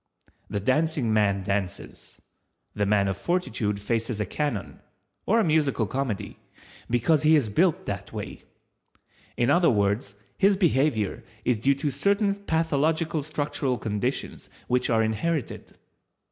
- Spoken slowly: Yes, slow, 125 wpm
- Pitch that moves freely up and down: Yes, wide, 7.1 semitones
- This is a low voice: Yes, low, 130 Hz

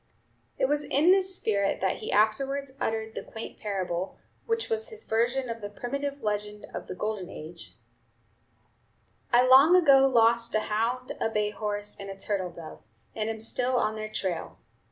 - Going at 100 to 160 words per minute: No, average, 175 wpm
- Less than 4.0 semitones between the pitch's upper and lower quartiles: No, average, 4.4 semitones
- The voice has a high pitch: Yes, high, 225 Hz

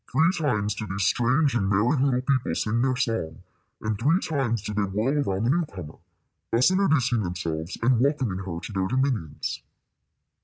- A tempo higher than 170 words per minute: Yes, average, 180 wpm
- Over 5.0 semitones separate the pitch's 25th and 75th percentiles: Yes, wide, 5.6 semitones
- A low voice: Yes, low, 115 Hz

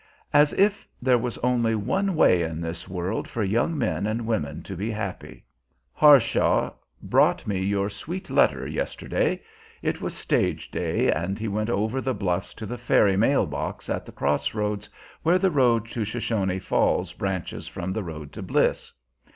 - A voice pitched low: Yes, low, 110 Hz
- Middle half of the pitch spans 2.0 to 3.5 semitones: No, average, 4.4 semitones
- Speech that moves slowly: No, average, 175 wpm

